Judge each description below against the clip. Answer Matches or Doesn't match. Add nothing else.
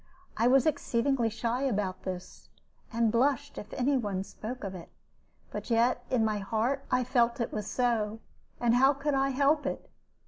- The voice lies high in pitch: Matches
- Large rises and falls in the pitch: Doesn't match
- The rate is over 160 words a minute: Matches